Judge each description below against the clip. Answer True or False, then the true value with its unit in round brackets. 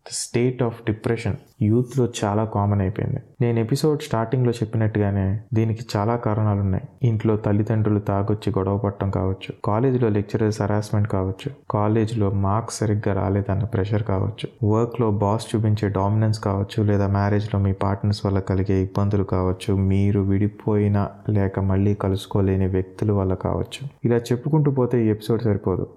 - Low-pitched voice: True (105 Hz)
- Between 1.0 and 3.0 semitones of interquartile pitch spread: True (2.4 semitones)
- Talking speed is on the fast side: True (150 wpm)